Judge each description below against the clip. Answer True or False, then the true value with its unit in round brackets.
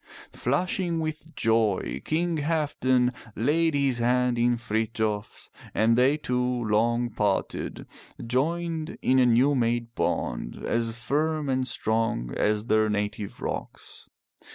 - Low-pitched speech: True (125 Hz)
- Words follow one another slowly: True (120 wpm)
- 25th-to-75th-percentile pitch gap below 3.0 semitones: False (4.5 semitones)